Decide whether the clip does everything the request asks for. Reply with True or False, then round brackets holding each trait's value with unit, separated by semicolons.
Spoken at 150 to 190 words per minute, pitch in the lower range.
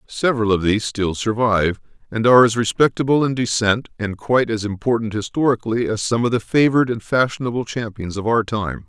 True (180 wpm; 115 Hz)